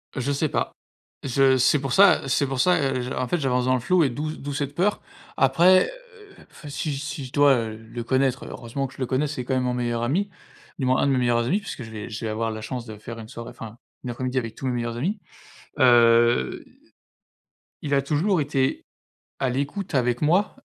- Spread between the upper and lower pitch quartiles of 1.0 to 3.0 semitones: No, average, 3.5 semitones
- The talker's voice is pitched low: Yes, low, 130 Hz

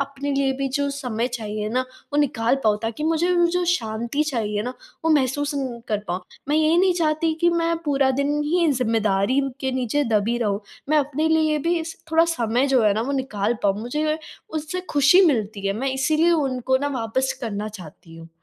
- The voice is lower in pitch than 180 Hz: No, very high, 270 Hz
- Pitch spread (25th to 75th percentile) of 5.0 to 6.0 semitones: Yes, average, 5.3 semitones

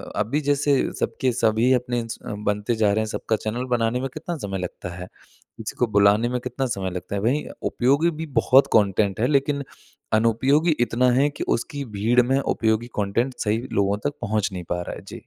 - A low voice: Yes, low, 115 Hz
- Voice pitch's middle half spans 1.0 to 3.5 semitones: No, average, 4.4 semitones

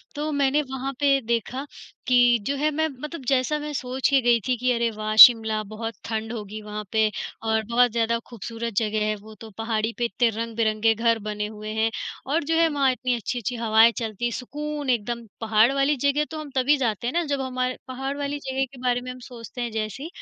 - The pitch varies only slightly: No, average, 3.5 semitones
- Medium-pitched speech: No, high, 240 Hz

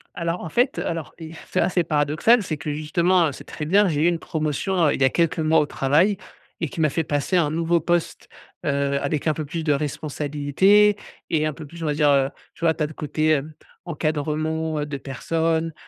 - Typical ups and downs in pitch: No, narrow, 2.3 semitones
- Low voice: No, medium, 155 Hz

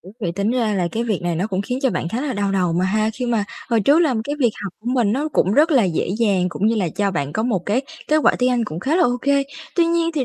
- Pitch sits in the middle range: No, high, 220 Hz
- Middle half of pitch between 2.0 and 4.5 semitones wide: No, wide, 5.4 semitones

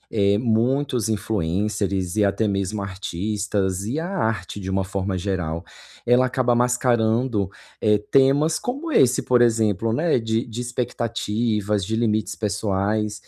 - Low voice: Yes, low, 110 Hz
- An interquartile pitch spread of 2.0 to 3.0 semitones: No, average, 3.5 semitones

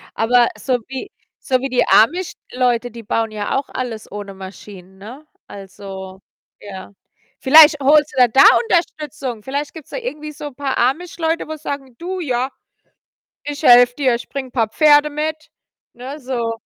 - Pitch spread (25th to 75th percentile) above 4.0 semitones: Yes, average, 4.6 semitones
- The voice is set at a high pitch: Yes, very high, 260 Hz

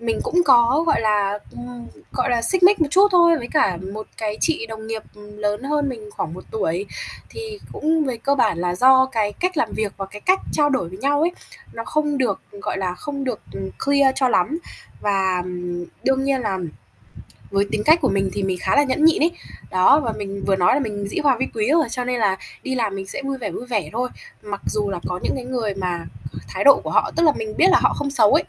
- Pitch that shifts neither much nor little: No, wide, 5.9 semitones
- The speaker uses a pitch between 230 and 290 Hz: Yes, high, 235 Hz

